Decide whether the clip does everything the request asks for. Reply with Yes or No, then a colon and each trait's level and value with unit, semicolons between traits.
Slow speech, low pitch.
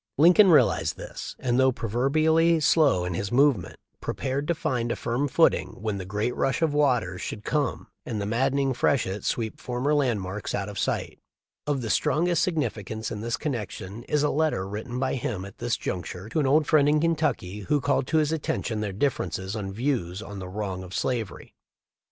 No: average, 195 wpm; low, 120 Hz